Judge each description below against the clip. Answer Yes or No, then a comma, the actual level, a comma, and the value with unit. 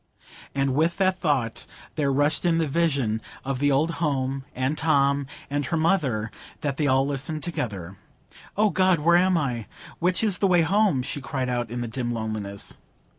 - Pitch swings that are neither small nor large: Yes, average, 4.6 semitones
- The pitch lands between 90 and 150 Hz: Yes, medium, 140 Hz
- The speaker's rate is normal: Yes, average, 175 wpm